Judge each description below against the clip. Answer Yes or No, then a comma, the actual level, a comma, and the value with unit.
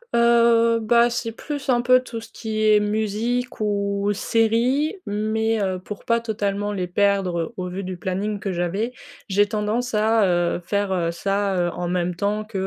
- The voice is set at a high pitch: Yes, high, 210 Hz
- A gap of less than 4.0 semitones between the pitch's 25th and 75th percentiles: Yes, average, 2.9 semitones